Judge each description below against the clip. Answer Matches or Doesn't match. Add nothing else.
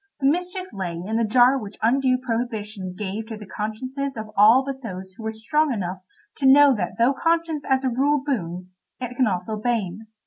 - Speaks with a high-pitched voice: Matches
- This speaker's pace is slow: Doesn't match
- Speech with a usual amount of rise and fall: Matches